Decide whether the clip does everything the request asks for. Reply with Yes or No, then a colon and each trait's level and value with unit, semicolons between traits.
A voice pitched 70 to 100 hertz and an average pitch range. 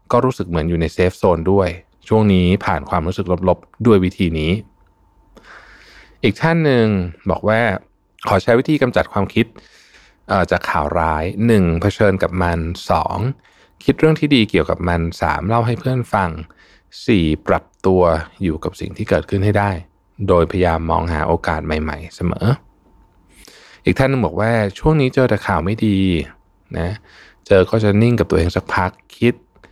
Yes: very low, 95 Hz; average, 4.4 semitones